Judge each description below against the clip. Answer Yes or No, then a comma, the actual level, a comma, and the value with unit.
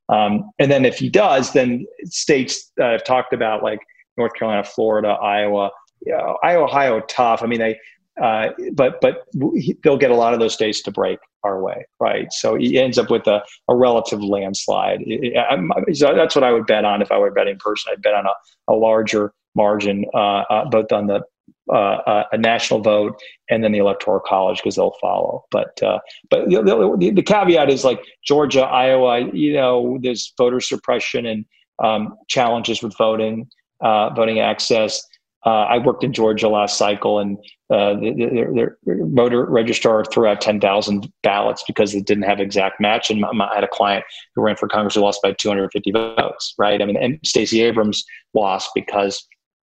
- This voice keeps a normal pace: Yes, average, 190 wpm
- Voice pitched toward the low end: Yes, low, 110 Hz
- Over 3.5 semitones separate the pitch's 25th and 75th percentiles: No, average, 3.1 semitones